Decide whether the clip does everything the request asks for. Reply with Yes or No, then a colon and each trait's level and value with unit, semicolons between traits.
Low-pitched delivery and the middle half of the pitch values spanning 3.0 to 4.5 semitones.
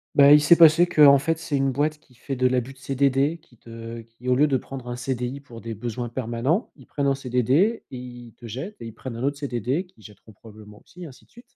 Yes: low, 130 Hz; average, 3.4 semitones